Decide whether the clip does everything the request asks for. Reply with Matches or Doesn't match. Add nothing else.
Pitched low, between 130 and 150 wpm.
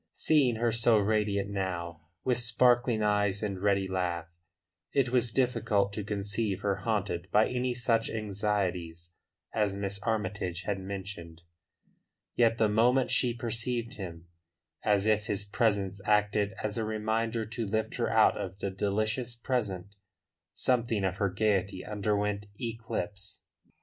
Matches